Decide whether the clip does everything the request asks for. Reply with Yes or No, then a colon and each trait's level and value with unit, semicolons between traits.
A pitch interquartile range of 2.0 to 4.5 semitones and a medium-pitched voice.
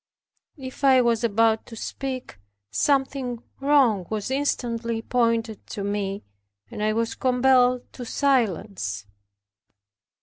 No: average, 3.3 semitones; high, 235 Hz